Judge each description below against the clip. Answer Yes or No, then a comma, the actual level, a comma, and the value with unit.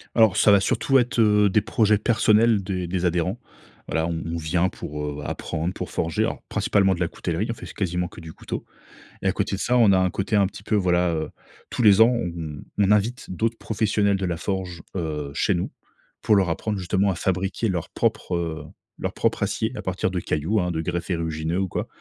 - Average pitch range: Yes, average, 3.6 semitones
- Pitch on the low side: Yes, very low, 95 Hz